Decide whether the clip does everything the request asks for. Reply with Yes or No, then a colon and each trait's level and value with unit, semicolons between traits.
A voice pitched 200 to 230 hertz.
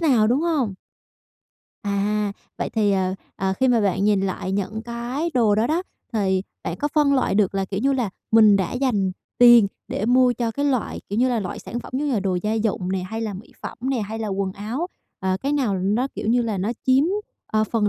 Yes: high, 220 Hz